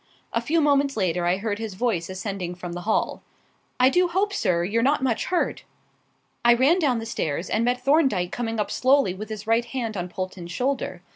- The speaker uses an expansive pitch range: Yes, wide, 6.2 semitones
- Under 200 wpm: No, fast, 205 wpm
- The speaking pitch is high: Yes, high, 225 Hz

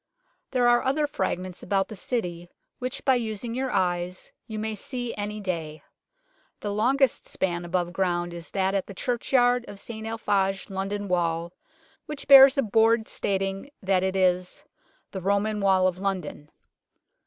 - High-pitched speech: Yes, high, 200 Hz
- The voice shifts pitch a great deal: No, average, 4.1 semitones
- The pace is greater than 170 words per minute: No, average, 160 wpm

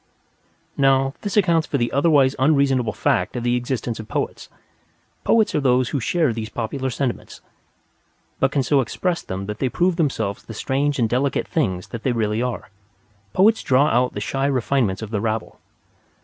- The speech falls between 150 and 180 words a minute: Yes, average, 175 wpm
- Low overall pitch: Yes, low, 130 Hz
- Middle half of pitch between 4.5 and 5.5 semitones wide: No, average, 3.8 semitones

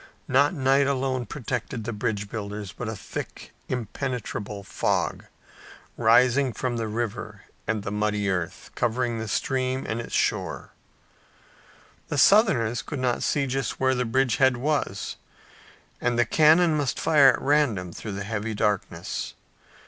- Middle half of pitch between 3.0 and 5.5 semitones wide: Yes, average, 4.0 semitones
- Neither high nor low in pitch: No, low, 120 Hz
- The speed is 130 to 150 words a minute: Yes, average, 145 wpm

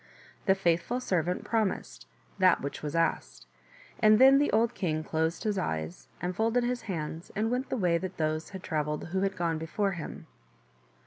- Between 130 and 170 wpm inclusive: No, average, 180 wpm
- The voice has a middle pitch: Yes, medium, 180 Hz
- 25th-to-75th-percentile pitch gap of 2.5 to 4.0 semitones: No, wide, 5.4 semitones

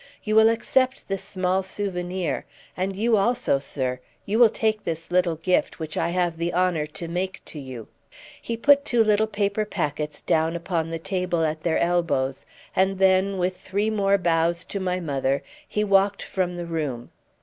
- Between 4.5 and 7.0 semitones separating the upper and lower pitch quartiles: No, average, 3.4 semitones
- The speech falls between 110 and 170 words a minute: No, average, 180 wpm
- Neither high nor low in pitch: Yes, medium, 180 Hz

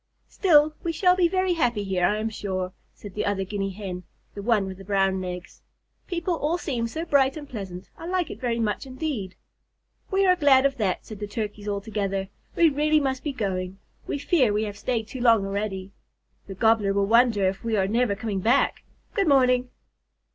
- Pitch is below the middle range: No, high, 220 Hz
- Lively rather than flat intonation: Yes, wide, 6.1 semitones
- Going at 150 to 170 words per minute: No, fast, 205 wpm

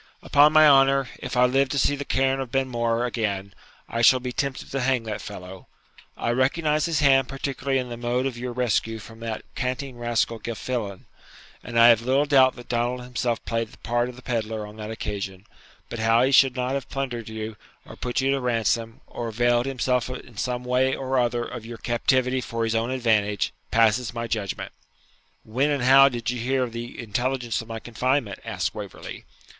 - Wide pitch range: No, narrow, 2.4 semitones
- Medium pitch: No, low, 120 Hz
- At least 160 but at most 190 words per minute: No, average, 200 wpm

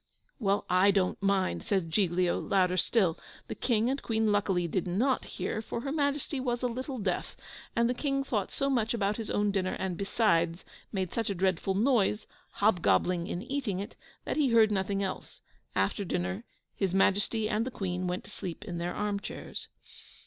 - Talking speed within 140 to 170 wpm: No, average, 190 wpm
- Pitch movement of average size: Yes, average, 4.0 semitones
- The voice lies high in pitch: Yes, high, 200 Hz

